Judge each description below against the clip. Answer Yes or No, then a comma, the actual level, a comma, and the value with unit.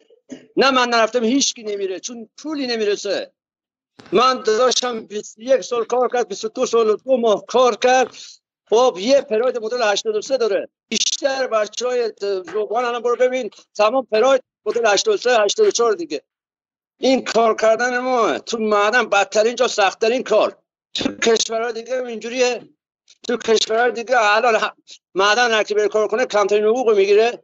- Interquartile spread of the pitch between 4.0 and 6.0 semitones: No, average, 3.0 semitones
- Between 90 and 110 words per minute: No, average, 150 wpm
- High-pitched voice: Yes, high, 240 Hz